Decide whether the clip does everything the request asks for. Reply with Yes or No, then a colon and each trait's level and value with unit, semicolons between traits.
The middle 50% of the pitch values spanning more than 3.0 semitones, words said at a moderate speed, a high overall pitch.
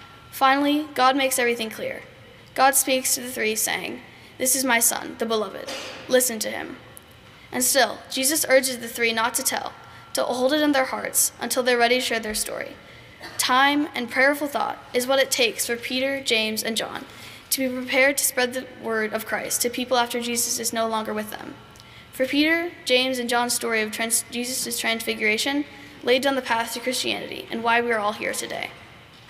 No: narrow, 2.6 semitones; average, 195 wpm; very high, 250 Hz